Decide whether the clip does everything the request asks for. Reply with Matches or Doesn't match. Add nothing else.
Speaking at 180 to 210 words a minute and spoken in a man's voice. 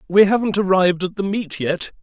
Matches